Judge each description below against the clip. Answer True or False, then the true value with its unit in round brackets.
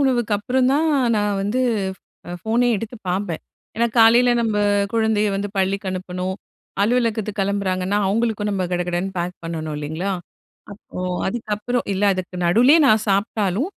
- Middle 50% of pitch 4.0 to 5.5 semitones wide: False (3.5 semitones)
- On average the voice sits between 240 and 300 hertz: False (205 Hz)